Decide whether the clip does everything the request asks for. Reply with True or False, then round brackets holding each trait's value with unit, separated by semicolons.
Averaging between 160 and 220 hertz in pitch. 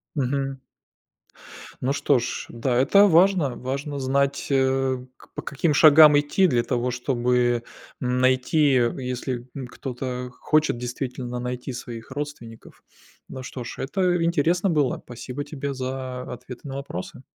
False (130 Hz)